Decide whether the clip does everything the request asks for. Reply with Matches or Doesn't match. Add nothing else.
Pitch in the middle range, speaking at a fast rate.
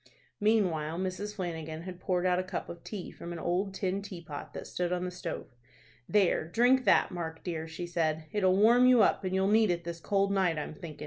Matches